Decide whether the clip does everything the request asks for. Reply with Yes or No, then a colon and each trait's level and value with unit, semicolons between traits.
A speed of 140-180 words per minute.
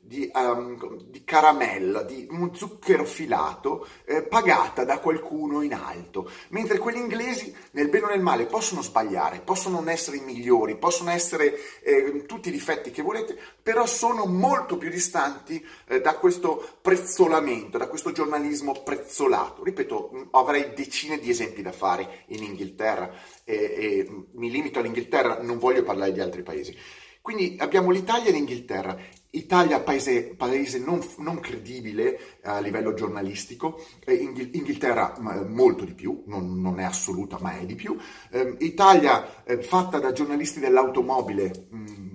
Yes: average, 150 wpm